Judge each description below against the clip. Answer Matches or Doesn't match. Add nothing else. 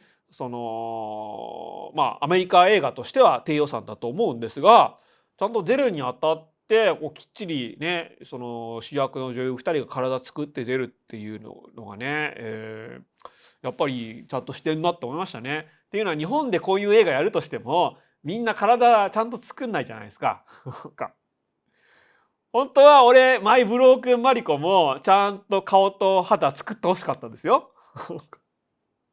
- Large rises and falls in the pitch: Matches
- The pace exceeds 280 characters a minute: Matches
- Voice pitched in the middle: Matches